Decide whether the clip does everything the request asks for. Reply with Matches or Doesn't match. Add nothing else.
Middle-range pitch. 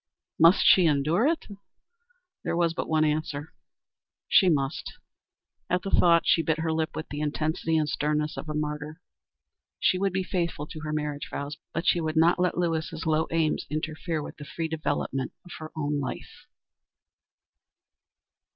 Matches